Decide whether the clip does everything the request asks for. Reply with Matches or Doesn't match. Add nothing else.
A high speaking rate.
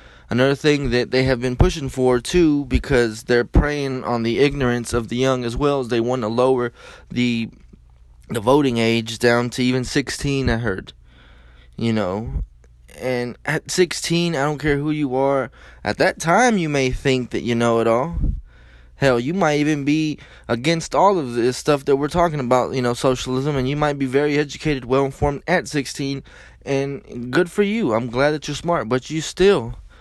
Doesn't match